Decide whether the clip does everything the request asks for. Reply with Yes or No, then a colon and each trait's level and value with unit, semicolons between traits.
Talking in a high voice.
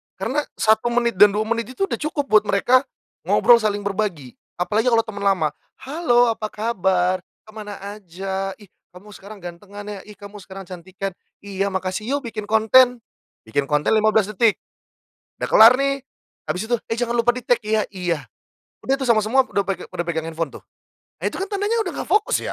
Yes: high, 215 Hz